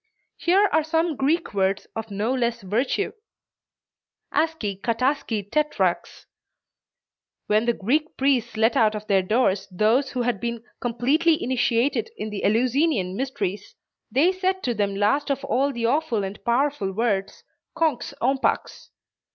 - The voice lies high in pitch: Yes, high, 240 Hz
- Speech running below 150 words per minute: Yes, average, 140 wpm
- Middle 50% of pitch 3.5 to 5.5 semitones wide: Yes, average, 5.1 semitones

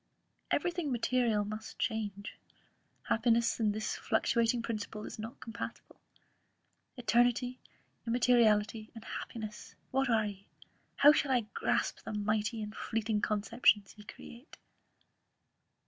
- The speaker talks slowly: Yes, slow, 115 wpm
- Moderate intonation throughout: No, narrow, 2.3 semitones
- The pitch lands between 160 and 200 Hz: No, high, 225 Hz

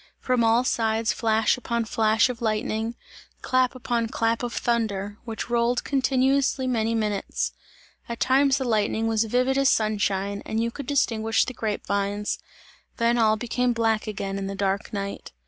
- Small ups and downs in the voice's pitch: Yes, narrow, 2.3 semitones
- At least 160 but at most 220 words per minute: Yes, average, 165 wpm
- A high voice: Yes, high, 225 Hz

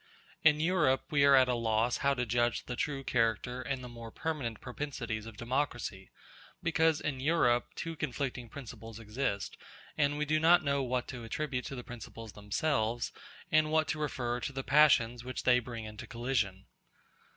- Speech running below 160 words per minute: No, average, 175 wpm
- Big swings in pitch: No, average, 3.9 semitones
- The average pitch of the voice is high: No, low, 125 Hz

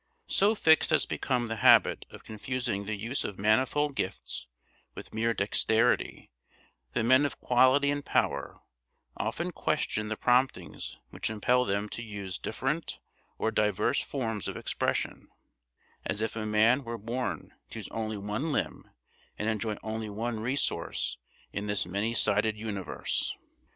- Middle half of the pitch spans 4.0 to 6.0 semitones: No, average, 3.3 semitones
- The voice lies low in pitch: Yes, low, 110 Hz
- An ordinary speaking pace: Yes, average, 145 wpm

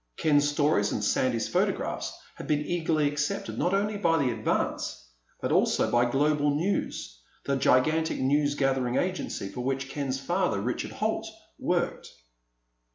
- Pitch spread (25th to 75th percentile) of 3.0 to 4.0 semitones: Yes, average, 3.7 semitones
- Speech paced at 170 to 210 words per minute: No, average, 145 wpm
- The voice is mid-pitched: Yes, medium, 145 Hz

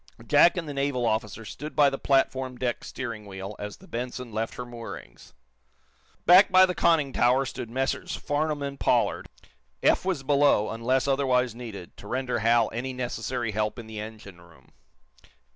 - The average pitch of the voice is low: Yes, low, 125 Hz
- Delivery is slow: No, average, 170 wpm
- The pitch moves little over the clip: No, average, 3.8 semitones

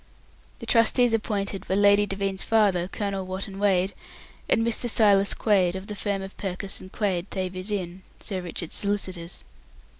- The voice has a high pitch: Yes, high, 195 Hz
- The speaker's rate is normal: Yes, average, 155 wpm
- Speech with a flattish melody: Yes, narrow, 1.7 semitones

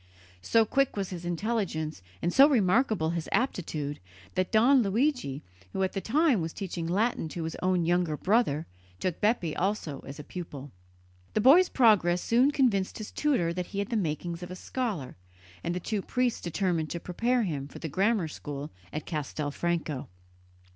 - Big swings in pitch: Yes, wide, 5.9 semitones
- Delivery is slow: No, average, 170 wpm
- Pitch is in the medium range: Yes, medium, 180 Hz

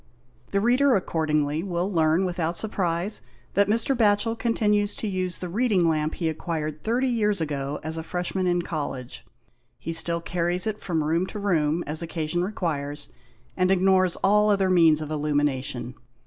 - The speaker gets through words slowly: No, average, 160 wpm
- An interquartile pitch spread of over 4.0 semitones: Yes, average, 4.4 semitones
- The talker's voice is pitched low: No, medium, 175 Hz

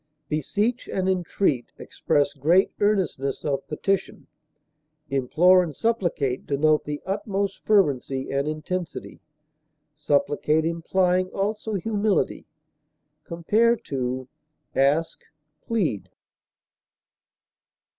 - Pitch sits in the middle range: Yes, medium, 170 Hz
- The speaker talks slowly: Yes, slow, 80 wpm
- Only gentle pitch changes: No, average, 5.2 semitones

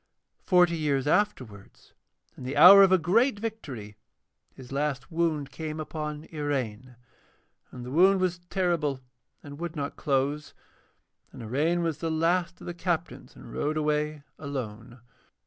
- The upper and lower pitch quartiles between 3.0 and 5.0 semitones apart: Yes, average, 4.1 semitones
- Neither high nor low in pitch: Yes, medium, 150 Hz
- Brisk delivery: No, average, 145 wpm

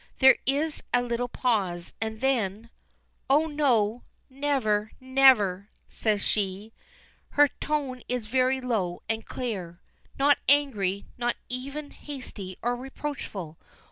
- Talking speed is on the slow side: Yes, slow, 115 wpm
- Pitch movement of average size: Yes, average, 4.6 semitones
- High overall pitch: Yes, high, 245 Hz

